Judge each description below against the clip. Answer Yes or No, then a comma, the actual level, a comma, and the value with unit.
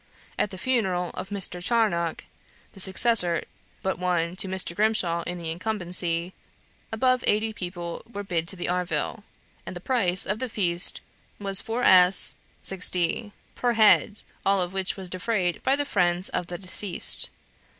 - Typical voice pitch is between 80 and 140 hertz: No, medium, 185 Hz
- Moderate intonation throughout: Yes, average, 3.3 semitones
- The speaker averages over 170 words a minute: No, average, 160 wpm